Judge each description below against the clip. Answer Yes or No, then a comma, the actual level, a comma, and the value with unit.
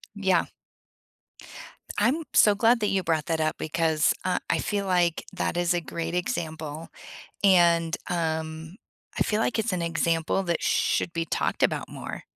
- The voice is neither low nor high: Yes, medium, 170 Hz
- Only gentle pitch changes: No, average, 3.1 semitones